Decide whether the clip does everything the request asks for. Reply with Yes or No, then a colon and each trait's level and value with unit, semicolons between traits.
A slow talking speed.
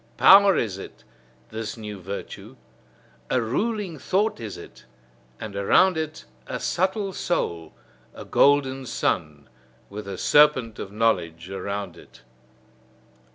Yes: slow, 120 wpm